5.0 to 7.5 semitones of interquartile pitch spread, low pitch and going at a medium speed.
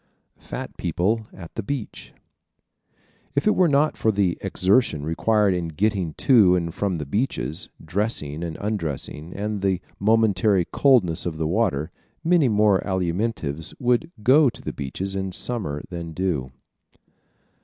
Yes: average, 5.3 semitones; very low, 95 Hz; average, 145 wpm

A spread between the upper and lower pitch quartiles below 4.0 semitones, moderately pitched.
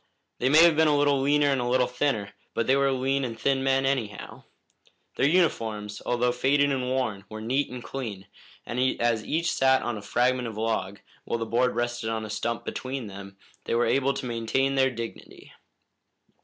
No: average, 3.2 semitones; low, 125 Hz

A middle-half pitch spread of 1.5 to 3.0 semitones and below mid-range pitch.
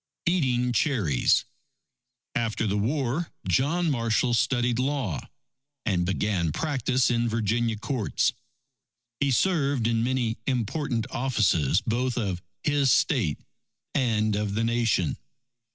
No: average, 3.7 semitones; low, 120 Hz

